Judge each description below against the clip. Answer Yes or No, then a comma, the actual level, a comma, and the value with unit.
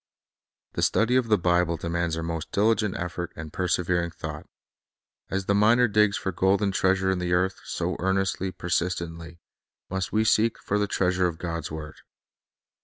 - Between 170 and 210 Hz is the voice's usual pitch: No, very low, 90 Hz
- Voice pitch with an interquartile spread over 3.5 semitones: No, average, 2.8 semitones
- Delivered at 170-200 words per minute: Yes, average, 175 wpm